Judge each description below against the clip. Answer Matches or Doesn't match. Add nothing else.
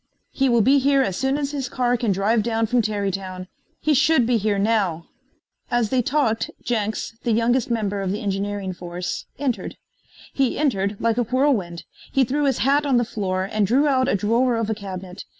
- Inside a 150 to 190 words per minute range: Doesn't match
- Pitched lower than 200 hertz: Doesn't match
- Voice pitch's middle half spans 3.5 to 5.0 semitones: Matches